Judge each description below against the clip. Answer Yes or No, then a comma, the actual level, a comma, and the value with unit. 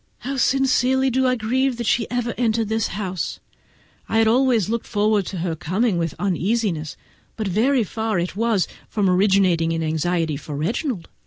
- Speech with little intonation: No, average, 5.1 semitones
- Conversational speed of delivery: Yes, average, 165 wpm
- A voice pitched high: Yes, high, 215 Hz